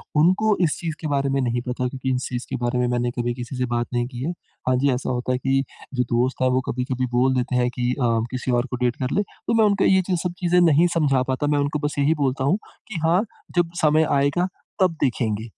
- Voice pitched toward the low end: Yes, low, 130 Hz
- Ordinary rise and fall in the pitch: Yes, average, 3.8 semitones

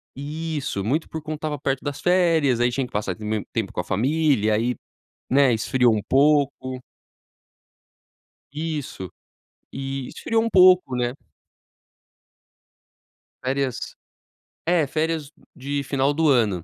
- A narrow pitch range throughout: No, average, 4.1 semitones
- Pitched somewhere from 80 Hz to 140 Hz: Yes, low, 135 Hz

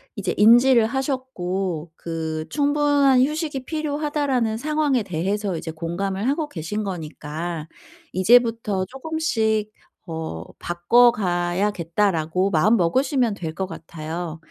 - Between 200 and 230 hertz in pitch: Yes, high, 205 Hz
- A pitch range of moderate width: No, wide, 7.3 semitones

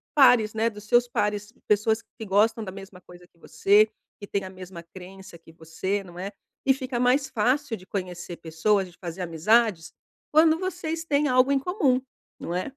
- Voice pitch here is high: Yes, high, 210 Hz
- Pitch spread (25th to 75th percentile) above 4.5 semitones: Yes, wide, 5.6 semitones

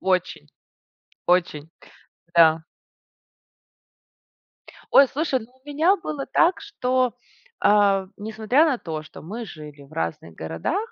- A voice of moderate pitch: No, high, 210 Hz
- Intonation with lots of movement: Yes, wide, 9.0 semitones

